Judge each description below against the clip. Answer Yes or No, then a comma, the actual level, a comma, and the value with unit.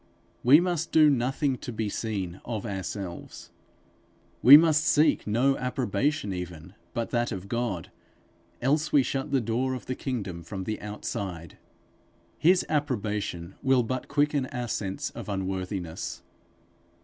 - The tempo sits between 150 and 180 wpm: No, slow, 135 wpm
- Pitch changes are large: Yes, wide, 5.8 semitones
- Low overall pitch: Yes, low, 120 Hz